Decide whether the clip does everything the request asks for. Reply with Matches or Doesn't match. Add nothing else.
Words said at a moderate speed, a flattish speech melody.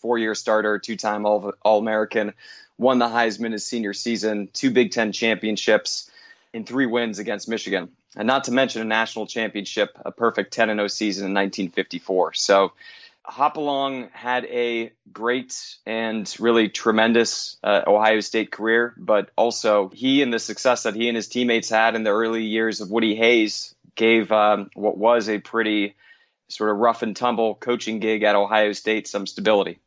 Matches